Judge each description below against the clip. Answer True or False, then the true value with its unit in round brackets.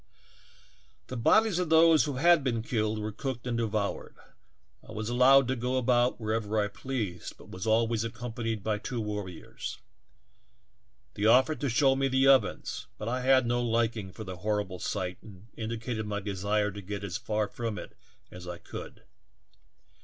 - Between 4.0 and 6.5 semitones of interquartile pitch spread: False (3.4 semitones)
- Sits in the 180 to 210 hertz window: False (115 Hz)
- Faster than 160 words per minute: True (170 wpm)